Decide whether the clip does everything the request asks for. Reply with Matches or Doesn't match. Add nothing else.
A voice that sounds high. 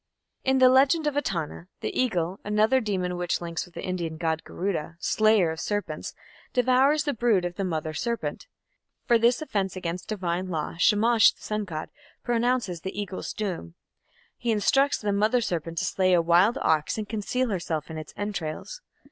Matches